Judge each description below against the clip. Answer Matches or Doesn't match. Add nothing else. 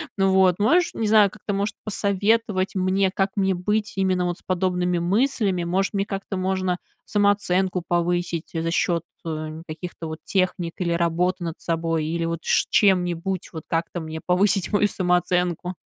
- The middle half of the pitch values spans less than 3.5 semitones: Matches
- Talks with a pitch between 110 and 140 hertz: Doesn't match